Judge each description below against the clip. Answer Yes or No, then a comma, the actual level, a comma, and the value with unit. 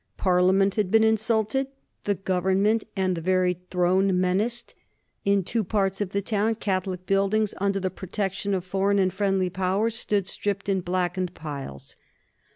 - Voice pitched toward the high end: Yes, high, 195 Hz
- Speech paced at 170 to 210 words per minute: No, average, 155 wpm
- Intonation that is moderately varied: No, narrow, 1.9 semitones